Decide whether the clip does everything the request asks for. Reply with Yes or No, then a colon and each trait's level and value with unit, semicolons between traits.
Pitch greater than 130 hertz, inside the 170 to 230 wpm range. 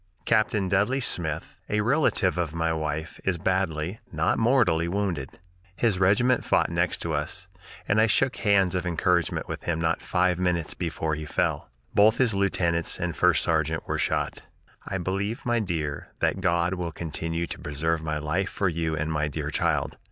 No: very low, 85 Hz; average, 175 wpm